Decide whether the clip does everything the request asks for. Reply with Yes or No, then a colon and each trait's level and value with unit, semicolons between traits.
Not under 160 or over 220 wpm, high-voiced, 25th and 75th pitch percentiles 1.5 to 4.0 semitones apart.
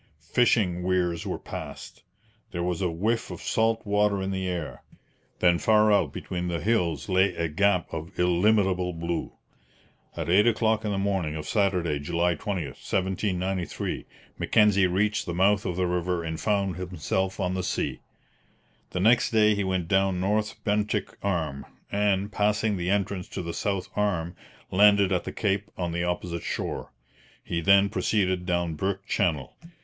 No: average, 165 wpm; very low, 95 Hz; average, 2.7 semitones